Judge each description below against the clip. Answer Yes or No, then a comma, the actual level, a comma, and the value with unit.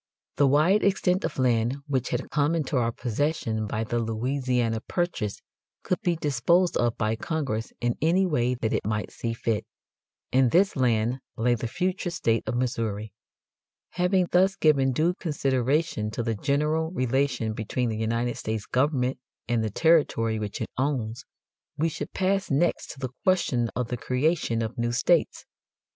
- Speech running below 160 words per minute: No, average, 165 wpm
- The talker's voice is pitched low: Yes, low, 130 Hz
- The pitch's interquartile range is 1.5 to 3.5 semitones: No, wide, 5.6 semitones